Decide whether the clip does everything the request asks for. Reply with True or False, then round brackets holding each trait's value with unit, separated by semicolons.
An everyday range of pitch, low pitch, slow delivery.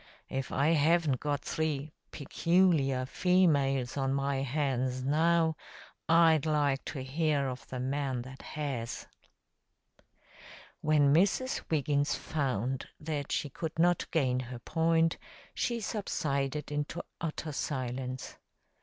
False (3.3 semitones; 145 Hz; 115 wpm)